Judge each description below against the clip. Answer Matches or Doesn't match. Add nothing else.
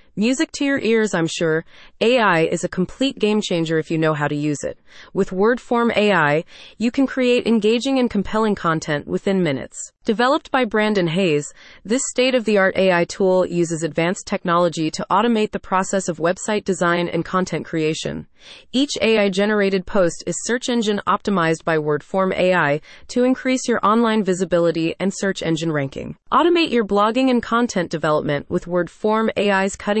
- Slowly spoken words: Doesn't match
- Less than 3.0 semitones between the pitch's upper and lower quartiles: Doesn't match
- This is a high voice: Matches